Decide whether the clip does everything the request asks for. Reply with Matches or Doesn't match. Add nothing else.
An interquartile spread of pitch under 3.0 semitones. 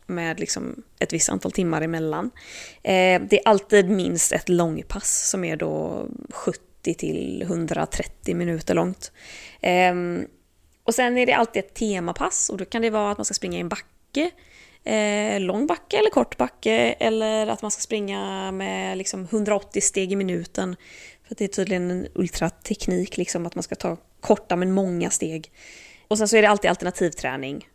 Doesn't match